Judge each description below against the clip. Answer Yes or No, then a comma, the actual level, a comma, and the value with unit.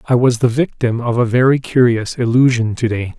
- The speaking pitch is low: Yes, low, 120 Hz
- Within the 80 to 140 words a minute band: No, fast, 205 wpm